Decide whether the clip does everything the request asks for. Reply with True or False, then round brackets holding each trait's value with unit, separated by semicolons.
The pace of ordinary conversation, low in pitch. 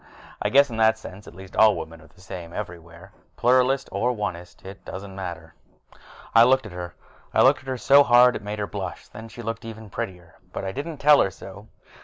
False (225 wpm; 105 Hz)